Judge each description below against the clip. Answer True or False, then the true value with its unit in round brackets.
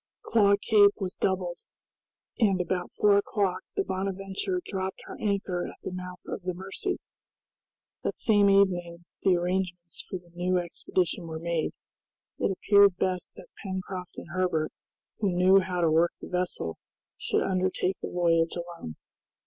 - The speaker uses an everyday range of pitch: False (1.8 semitones)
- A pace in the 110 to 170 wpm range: True (150 wpm)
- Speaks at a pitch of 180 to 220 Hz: True (185 Hz)